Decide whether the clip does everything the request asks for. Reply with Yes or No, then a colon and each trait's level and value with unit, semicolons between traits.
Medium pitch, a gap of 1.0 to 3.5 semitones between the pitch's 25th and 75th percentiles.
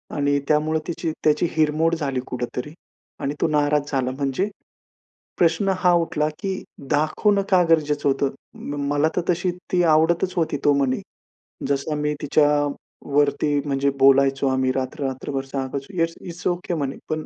Yes: medium, 150 Hz; average, 3.0 semitones